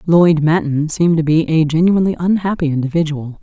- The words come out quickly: No, average, 160 wpm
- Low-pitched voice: No, medium, 160 Hz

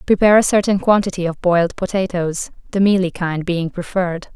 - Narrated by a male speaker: No, female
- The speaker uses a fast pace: No, average, 165 wpm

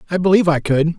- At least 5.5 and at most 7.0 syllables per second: No, 7.9 syllables/s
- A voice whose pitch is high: No, medium, 165 Hz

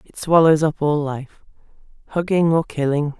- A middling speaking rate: Yes, average, 150 wpm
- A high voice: No, medium, 155 Hz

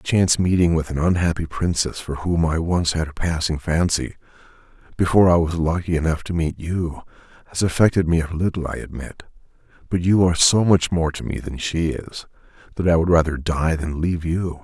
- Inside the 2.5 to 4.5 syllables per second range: No, 5.5 syllables/s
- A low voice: Yes, very low, 85 Hz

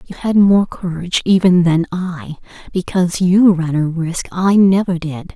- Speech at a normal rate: Yes, average, 170 wpm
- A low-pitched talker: No, medium, 180 Hz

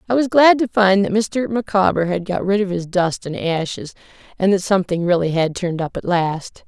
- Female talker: Yes, female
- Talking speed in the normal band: No, fast, 225 wpm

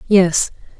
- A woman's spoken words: Yes, female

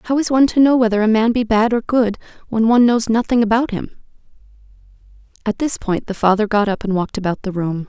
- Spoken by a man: No, female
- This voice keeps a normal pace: No, fast, 230 wpm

